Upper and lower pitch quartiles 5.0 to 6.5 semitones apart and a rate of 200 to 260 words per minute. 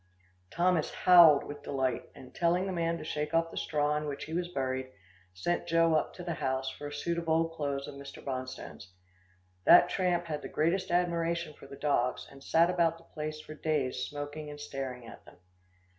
No: average, 3.3 semitones; fast, 205 wpm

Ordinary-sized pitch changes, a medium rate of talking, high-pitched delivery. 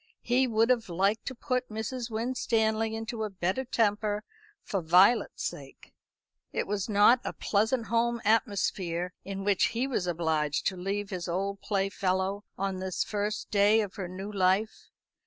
Yes: average, 3.0 semitones; average, 160 wpm; high, 205 Hz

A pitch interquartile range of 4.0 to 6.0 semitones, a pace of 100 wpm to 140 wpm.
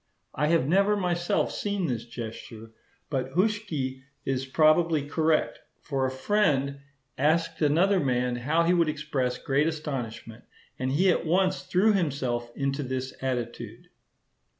Yes: average, 4.6 semitones; slow, 135 wpm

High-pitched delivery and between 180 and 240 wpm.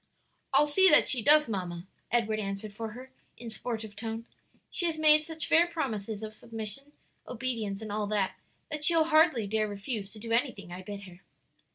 Yes: high, 225 Hz; average, 185 wpm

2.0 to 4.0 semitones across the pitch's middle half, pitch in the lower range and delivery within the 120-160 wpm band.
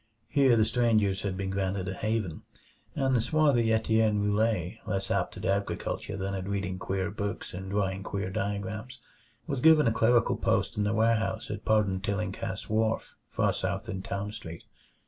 No: narrow, 2.6 semitones; low, 105 Hz; average, 170 wpm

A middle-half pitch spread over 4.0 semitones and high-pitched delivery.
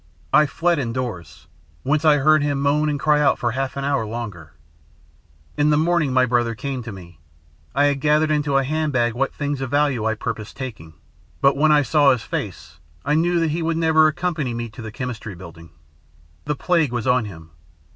No: average, 4.5 semitones; low, 135 Hz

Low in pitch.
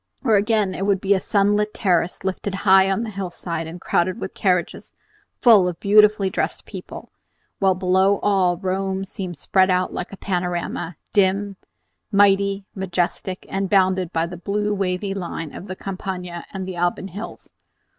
No: high, 190 Hz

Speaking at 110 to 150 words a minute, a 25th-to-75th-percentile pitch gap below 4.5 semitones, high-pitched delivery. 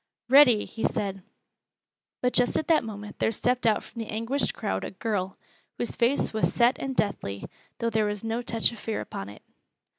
No: average, 190 wpm; average, 2.9 semitones; high, 225 Hz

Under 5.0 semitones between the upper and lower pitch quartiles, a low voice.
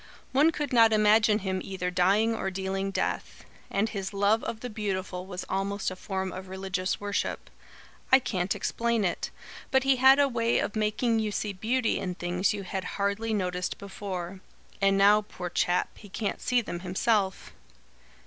No: average, 2.9 semitones; high, 200 Hz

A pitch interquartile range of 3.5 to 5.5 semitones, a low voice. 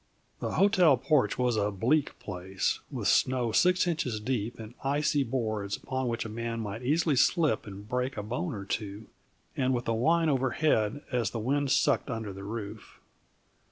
Yes: average, 4.6 semitones; low, 120 Hz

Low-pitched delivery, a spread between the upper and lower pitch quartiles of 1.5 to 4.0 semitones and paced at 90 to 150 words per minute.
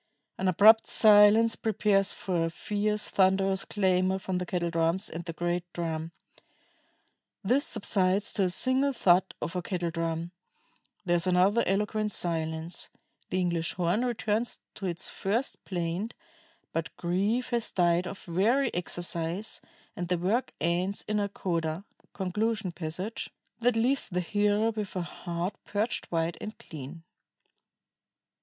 No: medium, 185 Hz; average, 3.6 semitones; average, 140 wpm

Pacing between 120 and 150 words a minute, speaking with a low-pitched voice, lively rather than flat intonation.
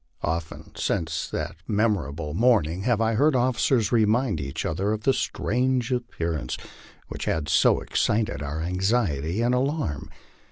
Yes: slow, 135 wpm; low, 105 Hz; wide, 7.1 semitones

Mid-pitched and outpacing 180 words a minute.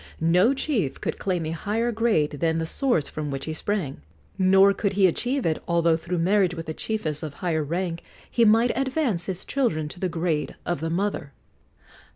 Yes: medium, 175 Hz; average, 190 wpm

